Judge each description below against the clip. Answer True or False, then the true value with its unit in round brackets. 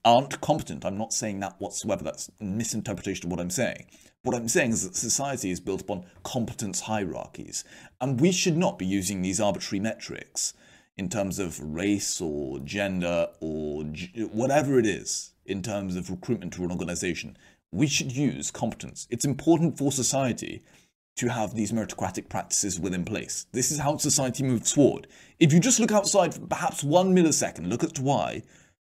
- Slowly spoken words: False (175 wpm)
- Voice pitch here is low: True (110 Hz)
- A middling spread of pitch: False (7.1 semitones)